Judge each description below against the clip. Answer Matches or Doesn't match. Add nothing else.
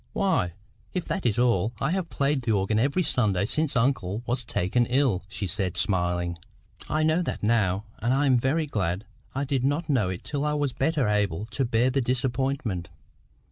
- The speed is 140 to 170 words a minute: Doesn't match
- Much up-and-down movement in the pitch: Matches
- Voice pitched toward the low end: Matches